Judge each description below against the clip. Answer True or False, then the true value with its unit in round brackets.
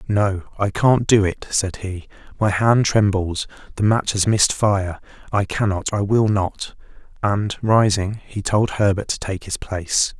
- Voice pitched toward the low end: True (100 Hz)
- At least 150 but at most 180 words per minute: True (170 wpm)